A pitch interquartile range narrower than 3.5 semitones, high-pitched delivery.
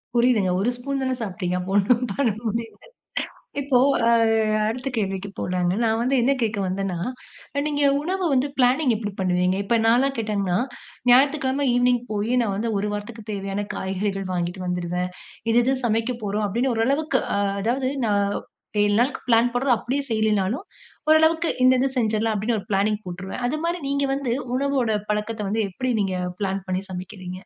No: average, 4.6 semitones; high, 220 Hz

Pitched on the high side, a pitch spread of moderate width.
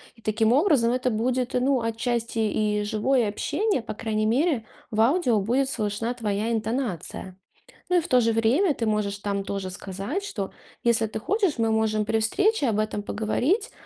Yes: high, 225 Hz; average, 3.3 semitones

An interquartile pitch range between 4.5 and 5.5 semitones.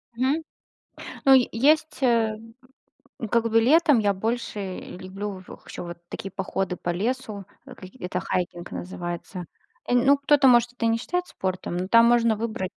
Yes: average, 5.2 semitones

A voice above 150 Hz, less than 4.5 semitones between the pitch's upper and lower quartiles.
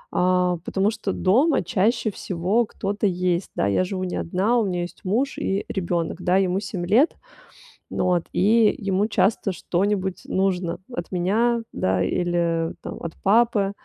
Yes: high, 190 Hz; average, 2.8 semitones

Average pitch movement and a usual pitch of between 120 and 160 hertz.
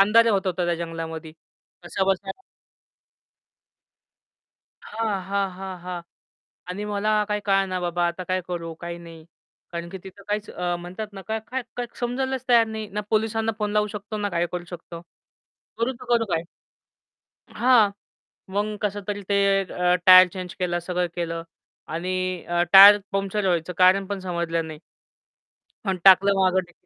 No: average, 3.0 semitones; high, 190 Hz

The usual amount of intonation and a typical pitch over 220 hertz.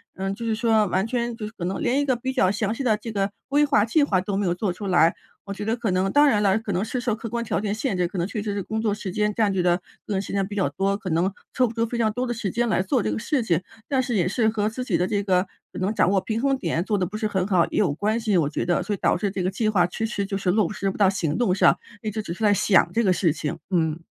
No: average, 3.3 semitones; high, 205 Hz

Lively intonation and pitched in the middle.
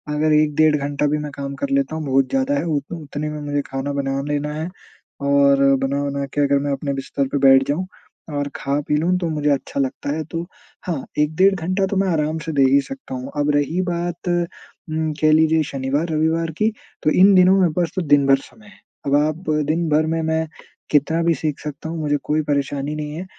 No: average, 2.7 semitones; medium, 150 Hz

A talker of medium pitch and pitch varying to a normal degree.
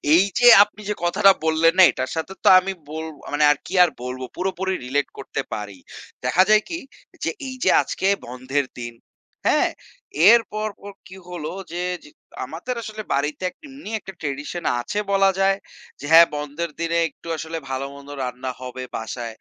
No: medium, 165 Hz; wide, 5.9 semitones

